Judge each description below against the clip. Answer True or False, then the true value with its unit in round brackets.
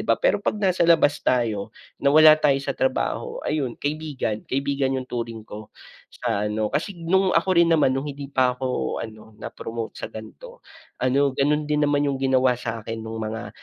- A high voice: False (135 Hz)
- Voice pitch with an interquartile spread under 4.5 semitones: False (4.8 semitones)